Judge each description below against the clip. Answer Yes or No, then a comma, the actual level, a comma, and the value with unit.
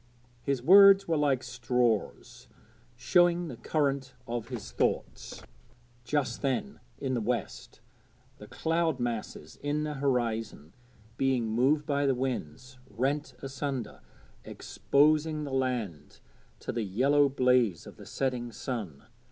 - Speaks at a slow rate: Yes, slow, 125 wpm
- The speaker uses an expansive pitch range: No, average, 3.5 semitones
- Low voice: Yes, low, 130 Hz